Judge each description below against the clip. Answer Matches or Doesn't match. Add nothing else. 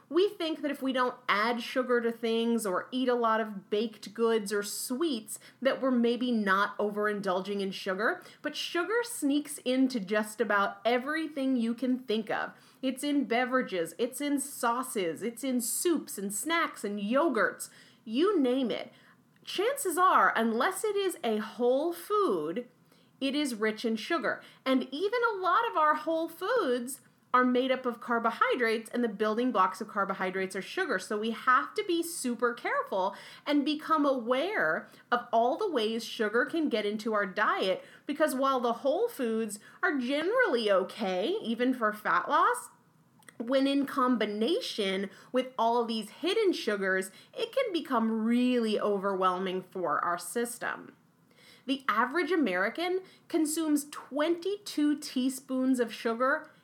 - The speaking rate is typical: Matches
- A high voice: Matches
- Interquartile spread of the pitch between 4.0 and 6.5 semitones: Matches